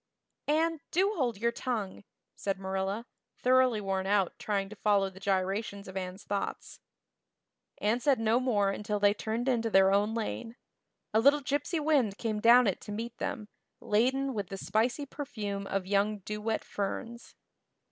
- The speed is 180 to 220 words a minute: No, average, 165 wpm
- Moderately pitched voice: No, high, 215 Hz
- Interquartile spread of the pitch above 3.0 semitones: Yes, average, 3.7 semitones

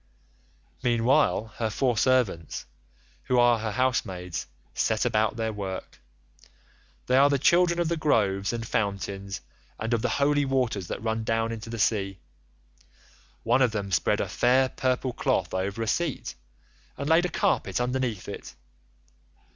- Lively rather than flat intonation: No, average, 4.0 semitones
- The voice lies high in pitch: No, low, 115 Hz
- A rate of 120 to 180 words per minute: Yes, average, 150 wpm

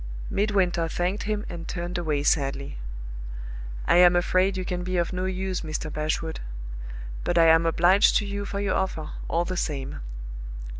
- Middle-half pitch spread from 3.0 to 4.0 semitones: No, narrow, 2.5 semitones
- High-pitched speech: No, medium, 175 Hz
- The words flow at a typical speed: Yes, average, 165 wpm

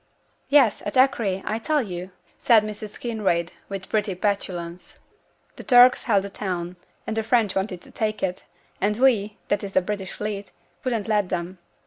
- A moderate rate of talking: Yes, average, 170 wpm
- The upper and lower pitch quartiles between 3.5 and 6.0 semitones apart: No, average, 2.8 semitones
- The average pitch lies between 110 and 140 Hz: No, high, 205 Hz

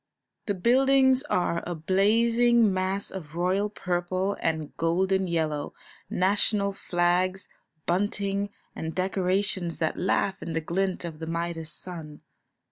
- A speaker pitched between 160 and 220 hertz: Yes, medium, 185 Hz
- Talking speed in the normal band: No, slow, 125 wpm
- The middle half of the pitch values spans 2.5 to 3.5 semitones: Yes, average, 2.9 semitones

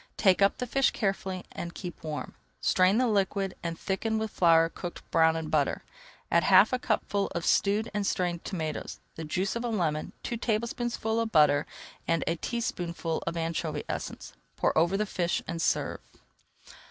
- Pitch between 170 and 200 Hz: Yes, medium, 185 Hz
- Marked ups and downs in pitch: No, average, 4.6 semitones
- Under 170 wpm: No, average, 175 wpm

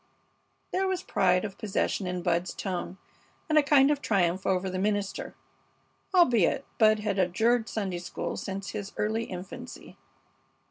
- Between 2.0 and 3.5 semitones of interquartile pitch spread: No, average, 3.9 semitones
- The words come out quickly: No, average, 145 wpm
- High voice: Yes, high, 200 Hz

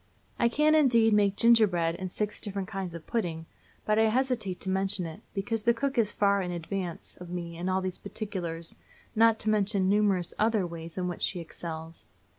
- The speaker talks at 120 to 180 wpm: No, average, 195 wpm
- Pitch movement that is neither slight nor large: Yes, average, 3.8 semitones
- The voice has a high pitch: Yes, high, 195 Hz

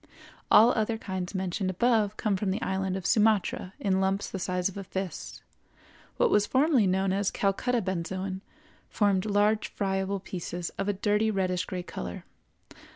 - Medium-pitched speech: No, high, 195 Hz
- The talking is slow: No, average, 160 wpm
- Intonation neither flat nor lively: No, narrow, 1.9 semitones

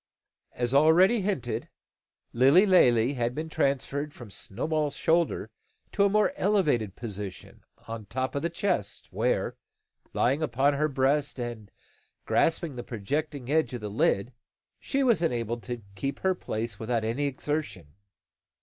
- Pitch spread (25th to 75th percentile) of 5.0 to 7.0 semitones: Yes, average, 5.3 semitones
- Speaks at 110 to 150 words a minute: Yes, average, 145 wpm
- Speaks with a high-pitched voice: No, low, 135 Hz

